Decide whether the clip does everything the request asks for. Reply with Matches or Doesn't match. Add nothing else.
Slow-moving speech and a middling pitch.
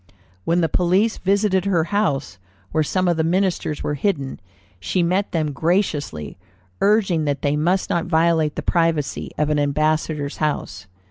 Doesn't match